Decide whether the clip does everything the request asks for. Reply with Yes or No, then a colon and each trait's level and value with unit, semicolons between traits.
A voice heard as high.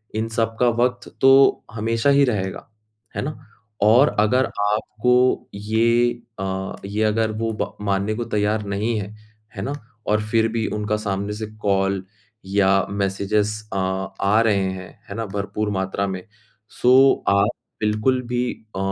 No: low, 105 Hz